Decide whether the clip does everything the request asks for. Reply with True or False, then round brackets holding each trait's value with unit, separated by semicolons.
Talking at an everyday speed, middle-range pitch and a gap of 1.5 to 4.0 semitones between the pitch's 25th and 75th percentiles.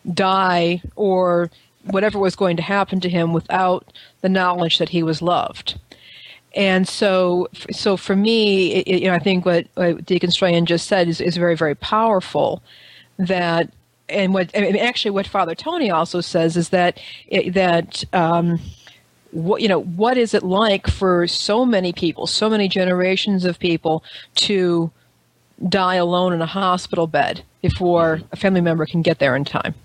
True (170 wpm; 180 Hz; 2.4 semitones)